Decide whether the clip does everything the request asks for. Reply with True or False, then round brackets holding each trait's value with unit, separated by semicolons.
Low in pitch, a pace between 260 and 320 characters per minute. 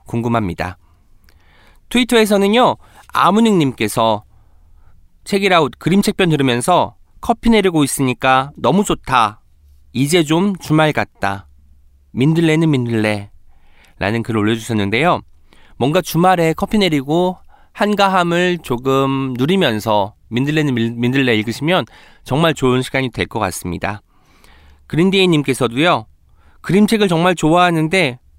True (130 Hz; 280 characters per minute)